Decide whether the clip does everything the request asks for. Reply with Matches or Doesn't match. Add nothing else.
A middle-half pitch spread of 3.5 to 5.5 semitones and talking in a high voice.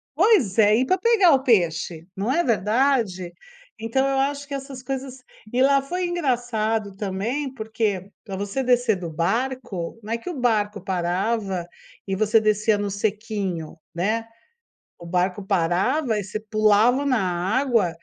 Matches